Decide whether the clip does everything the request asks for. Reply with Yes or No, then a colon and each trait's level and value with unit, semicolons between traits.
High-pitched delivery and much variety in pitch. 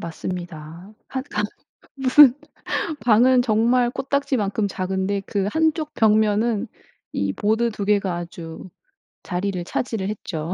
No: high, 210 Hz; average, 4.6 semitones